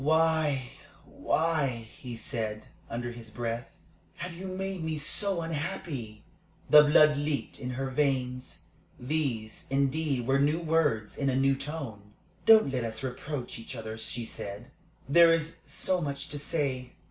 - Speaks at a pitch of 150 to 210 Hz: No, medium, 140 Hz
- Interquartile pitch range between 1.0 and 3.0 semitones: No, average, 4.7 semitones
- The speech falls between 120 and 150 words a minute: Yes, average, 145 wpm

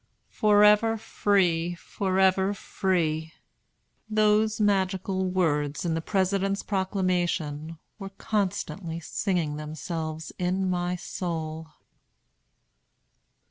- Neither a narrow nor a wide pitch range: Yes, average, 3.3 semitones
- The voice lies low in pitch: No, medium, 185 Hz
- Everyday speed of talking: No, slow, 80 wpm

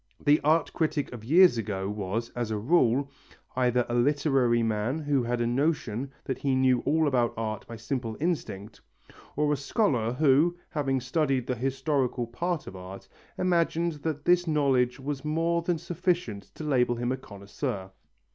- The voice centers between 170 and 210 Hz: No, low, 130 Hz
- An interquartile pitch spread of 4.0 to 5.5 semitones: Yes, average, 4.4 semitones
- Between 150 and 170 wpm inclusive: Yes, average, 165 wpm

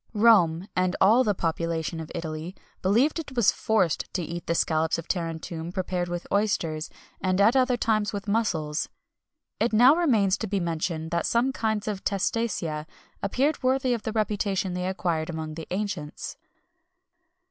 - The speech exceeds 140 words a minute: Yes, average, 160 wpm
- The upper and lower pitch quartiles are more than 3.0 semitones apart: Yes, average, 4.9 semitones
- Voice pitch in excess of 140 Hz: Yes, high, 190 Hz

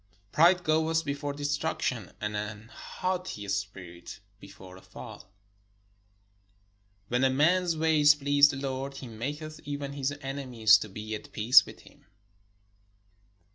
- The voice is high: No, low, 135 Hz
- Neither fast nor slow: No, slow, 130 wpm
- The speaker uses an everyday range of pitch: No, wide, 5.7 semitones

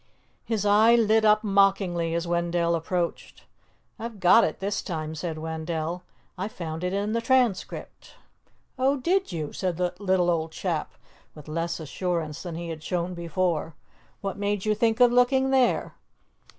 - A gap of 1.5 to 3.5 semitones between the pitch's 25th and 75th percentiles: No, average, 4.3 semitones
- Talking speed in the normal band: Yes, average, 160 wpm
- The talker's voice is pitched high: No, medium, 180 Hz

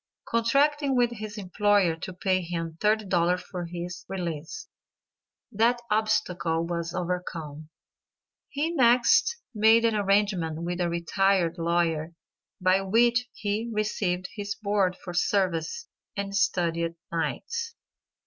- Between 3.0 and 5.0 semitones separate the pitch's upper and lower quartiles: Yes, average, 4.2 semitones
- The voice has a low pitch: No, high, 190 Hz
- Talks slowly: Yes, slow, 115 wpm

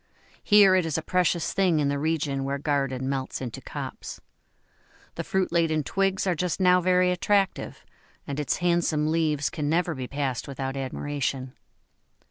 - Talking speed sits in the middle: Yes, average, 160 wpm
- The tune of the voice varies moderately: Yes, average, 4.5 semitones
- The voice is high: No, medium, 155 Hz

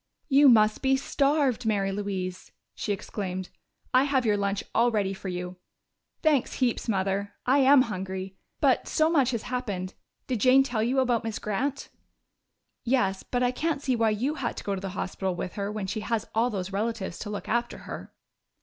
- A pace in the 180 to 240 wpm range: Yes, average, 190 wpm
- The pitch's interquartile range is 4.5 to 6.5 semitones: Yes, average, 4.8 semitones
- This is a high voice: Yes, high, 220 Hz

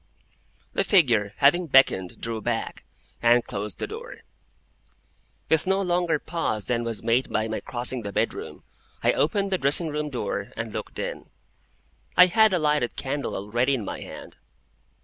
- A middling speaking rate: Yes, average, 160 wpm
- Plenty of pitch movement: Yes, wide, 7.0 semitones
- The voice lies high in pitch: No, low, 135 Hz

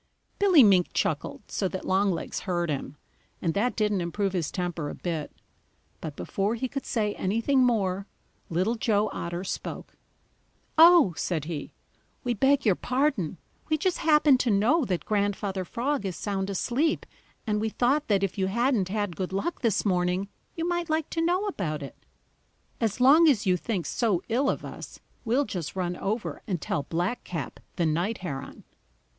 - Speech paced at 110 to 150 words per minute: No, average, 170 wpm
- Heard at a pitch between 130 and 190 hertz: No, high, 205 Hz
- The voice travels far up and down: Yes, wide, 5.9 semitones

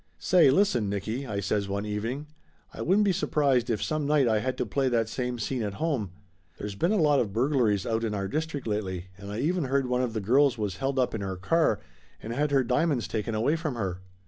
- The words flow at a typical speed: No, fast, 235 wpm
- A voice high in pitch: No, low, 120 Hz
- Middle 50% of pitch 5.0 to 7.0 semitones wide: Yes, average, 5.3 semitones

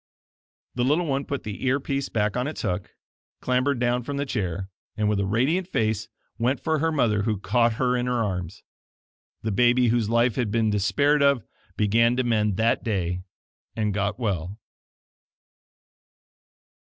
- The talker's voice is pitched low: Yes, low, 115 Hz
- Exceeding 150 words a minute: Yes, average, 165 wpm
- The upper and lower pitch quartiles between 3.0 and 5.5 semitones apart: Yes, average, 3.7 semitones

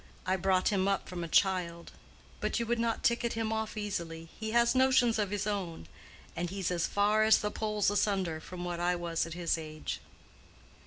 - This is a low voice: No, high, 195 Hz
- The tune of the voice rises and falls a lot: No, average, 4.0 semitones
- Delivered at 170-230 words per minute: Yes, average, 200 wpm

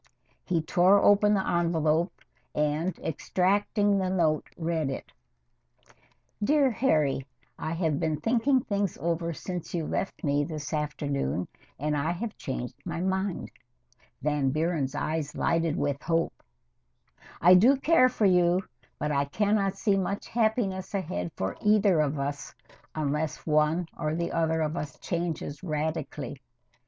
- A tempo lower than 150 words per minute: Yes, average, 140 wpm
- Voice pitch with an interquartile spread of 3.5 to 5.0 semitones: Yes, average, 4.3 semitones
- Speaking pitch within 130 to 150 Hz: No, medium, 165 Hz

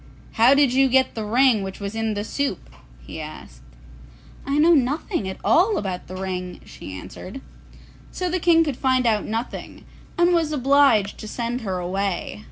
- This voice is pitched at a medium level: No, high, 235 Hz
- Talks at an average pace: Yes, average, 175 wpm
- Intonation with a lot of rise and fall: Yes, wide, 6.4 semitones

